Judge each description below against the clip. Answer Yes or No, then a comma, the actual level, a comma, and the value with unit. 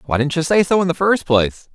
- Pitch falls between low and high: Yes, medium, 160 Hz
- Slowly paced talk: No, fast, 310 wpm